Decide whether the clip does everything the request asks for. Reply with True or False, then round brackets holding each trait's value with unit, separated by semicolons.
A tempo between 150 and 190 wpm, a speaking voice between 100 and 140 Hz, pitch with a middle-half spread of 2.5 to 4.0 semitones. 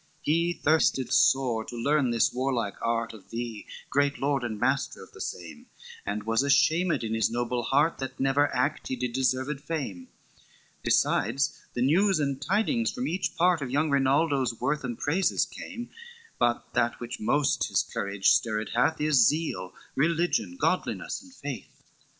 False (165 wpm; 135 Hz; 4.5 semitones)